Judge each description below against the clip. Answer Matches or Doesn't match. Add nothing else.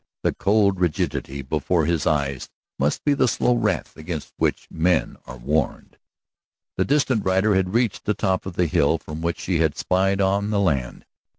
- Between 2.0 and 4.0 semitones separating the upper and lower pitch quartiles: Doesn't match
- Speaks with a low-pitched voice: Matches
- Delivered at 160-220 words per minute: Matches